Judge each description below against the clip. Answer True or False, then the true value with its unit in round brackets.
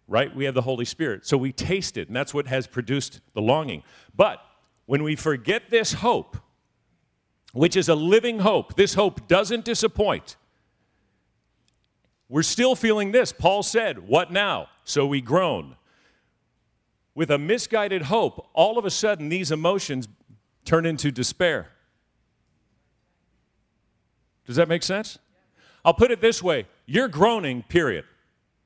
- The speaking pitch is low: False (165 Hz)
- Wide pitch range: True (7.4 semitones)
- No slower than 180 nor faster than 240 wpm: False (140 wpm)